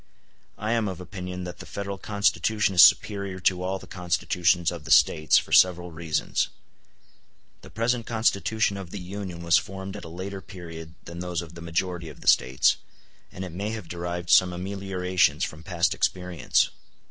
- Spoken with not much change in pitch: Yes, narrow, 2.3 semitones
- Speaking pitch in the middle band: No, very low, 90 Hz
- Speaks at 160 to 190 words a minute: Yes, average, 175 wpm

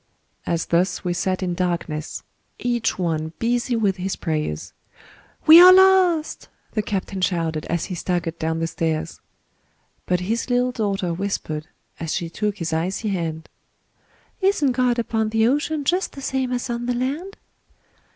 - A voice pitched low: No, high, 195 Hz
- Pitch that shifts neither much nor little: No, wide, 6.6 semitones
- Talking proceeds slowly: No, average, 155 wpm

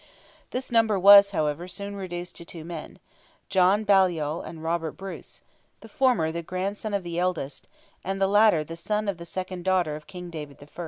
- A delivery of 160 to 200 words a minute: Yes, average, 170 wpm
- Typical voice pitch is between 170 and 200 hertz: Yes, medium, 185 Hz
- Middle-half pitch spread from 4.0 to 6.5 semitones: No, average, 3.2 semitones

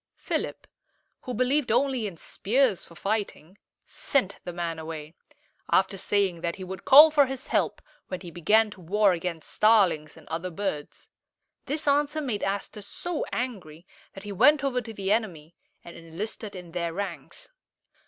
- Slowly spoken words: No, average, 165 wpm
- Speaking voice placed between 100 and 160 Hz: No, high, 200 Hz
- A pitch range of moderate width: No, wide, 6.4 semitones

